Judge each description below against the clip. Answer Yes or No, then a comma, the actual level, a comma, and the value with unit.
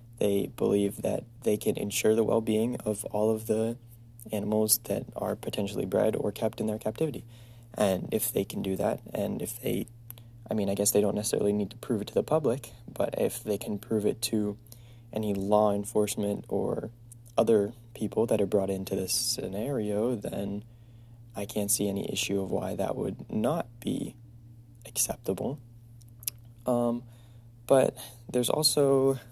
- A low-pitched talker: Yes, low, 115 Hz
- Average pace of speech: Yes, average, 165 wpm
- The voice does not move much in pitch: Yes, narrow, 2.0 semitones